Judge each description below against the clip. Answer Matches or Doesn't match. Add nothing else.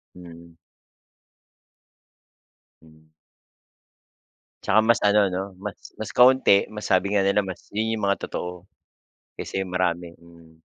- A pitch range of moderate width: Matches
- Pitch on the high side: Doesn't match